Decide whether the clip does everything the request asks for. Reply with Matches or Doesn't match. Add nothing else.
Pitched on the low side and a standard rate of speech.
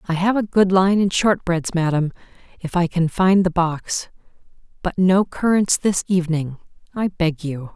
Doesn't match